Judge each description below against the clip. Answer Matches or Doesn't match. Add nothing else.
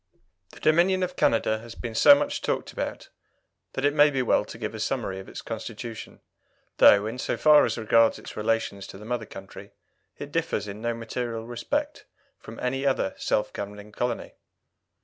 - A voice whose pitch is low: Matches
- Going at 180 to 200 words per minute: Matches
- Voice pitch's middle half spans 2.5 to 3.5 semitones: Doesn't match